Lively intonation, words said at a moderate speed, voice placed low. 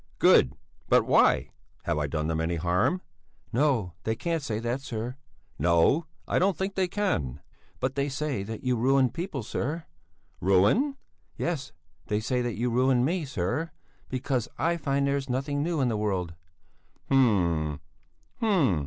Yes: wide, 6.6 semitones; average, 160 wpm; low, 130 Hz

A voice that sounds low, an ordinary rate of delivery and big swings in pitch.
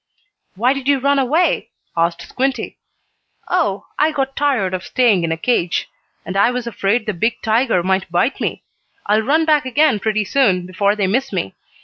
No: high, 225 Hz; average, 180 wpm; wide, 6.1 semitones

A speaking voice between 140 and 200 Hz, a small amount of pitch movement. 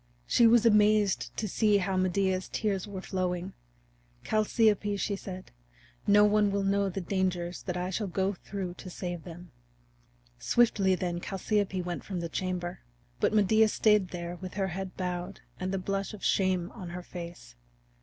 Yes: high, 190 Hz; narrow, 2.3 semitones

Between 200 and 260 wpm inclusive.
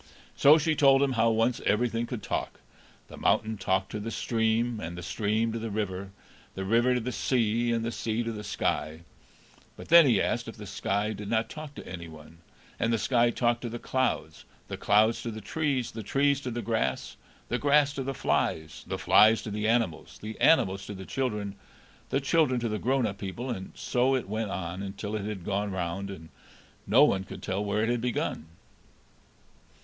Yes: fast, 205 wpm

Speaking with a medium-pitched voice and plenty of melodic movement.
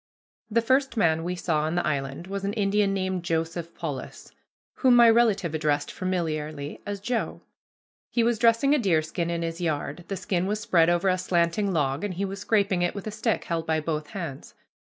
No: medium, 180 Hz; average, 4.1 semitones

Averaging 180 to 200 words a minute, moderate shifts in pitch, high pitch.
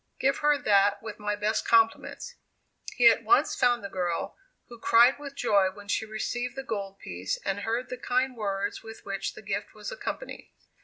Yes: average, 190 wpm; average, 3.7 semitones; high, 225 Hz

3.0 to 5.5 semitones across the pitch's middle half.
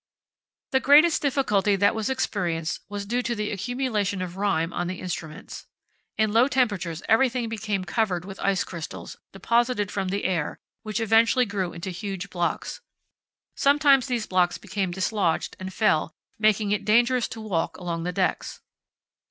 Yes: average, 4.1 semitones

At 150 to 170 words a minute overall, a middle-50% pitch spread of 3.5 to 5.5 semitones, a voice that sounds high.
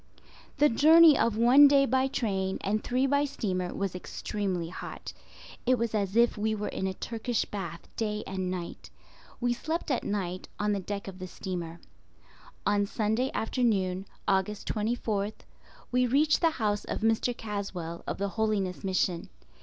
Yes: average, 160 wpm; average, 4.2 semitones; high, 210 Hz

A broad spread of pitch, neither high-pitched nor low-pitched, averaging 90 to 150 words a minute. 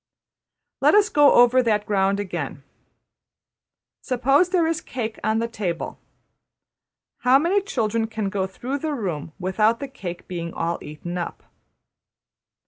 No: wide, 6.2 semitones; high, 220 Hz; average, 145 wpm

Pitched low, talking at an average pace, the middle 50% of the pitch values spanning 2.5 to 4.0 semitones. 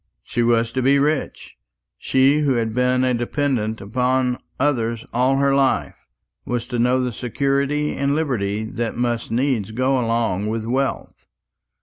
Yes: low, 125 Hz; average, 150 wpm; average, 2.9 semitones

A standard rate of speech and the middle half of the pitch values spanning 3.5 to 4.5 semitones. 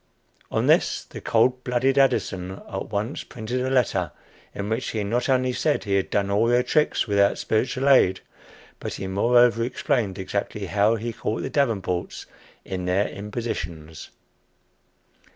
Yes: average, 150 wpm; average, 4.1 semitones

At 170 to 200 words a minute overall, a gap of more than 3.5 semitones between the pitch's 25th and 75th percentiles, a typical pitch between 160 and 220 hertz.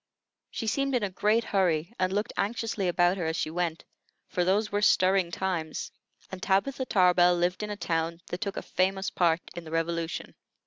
No: average, 190 wpm; average, 3.1 semitones; medium, 185 Hz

